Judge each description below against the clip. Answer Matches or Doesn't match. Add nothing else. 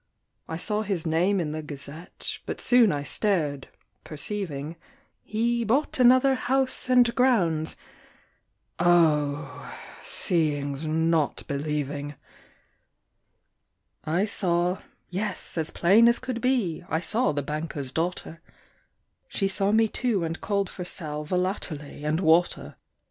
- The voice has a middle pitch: Matches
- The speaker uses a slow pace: Matches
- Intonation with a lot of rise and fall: Matches